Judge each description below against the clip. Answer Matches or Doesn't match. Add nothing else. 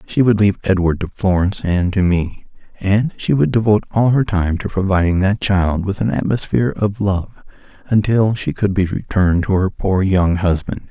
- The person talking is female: Doesn't match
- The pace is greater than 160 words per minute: Matches